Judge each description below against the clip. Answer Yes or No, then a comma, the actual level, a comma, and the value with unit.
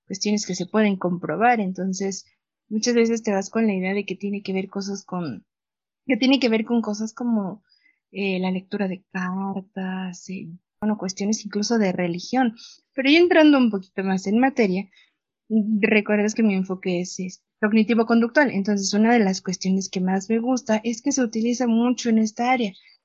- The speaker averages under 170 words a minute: No, average, 185 wpm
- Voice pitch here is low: No, high, 210 Hz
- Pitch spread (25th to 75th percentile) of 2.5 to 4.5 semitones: Yes, average, 3.5 semitones